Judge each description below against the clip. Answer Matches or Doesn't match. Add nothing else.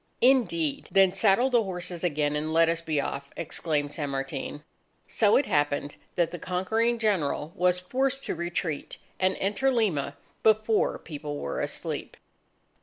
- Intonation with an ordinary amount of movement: Doesn't match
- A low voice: Doesn't match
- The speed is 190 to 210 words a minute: Doesn't match